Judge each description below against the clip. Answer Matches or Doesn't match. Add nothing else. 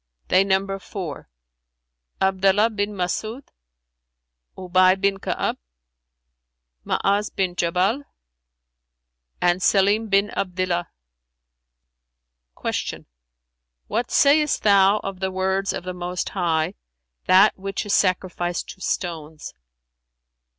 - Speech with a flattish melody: Matches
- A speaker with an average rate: Doesn't match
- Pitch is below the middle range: Doesn't match